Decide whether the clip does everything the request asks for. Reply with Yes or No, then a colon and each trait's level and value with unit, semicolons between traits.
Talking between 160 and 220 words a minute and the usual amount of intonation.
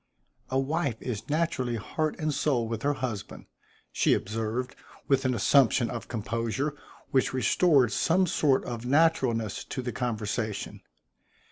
No: slow, 135 wpm; average, 4.0 semitones